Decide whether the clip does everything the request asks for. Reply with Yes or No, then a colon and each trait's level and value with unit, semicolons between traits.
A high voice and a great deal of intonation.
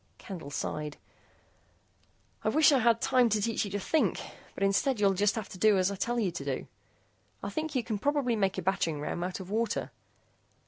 No: high, 205 Hz; average, 4.0 semitones